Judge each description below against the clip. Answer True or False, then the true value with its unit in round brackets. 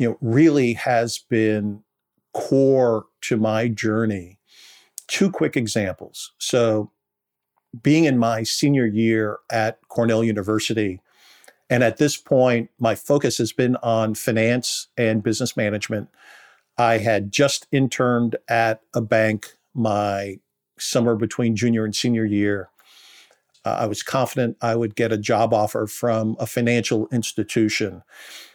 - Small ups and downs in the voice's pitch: True (1.9 semitones)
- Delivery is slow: True (130 wpm)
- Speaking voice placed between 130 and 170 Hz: False (115 Hz)